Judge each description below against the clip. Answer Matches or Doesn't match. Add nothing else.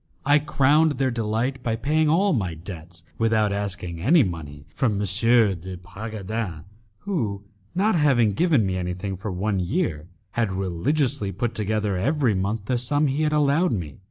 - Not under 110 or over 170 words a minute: Matches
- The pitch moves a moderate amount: Doesn't match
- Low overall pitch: Matches